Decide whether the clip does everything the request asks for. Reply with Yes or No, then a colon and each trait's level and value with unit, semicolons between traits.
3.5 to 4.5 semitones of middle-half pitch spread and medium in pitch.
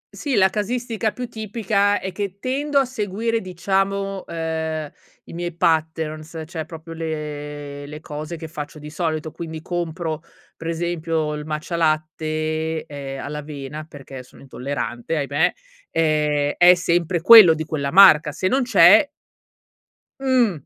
Yes: average, 3.9 semitones; medium, 160 Hz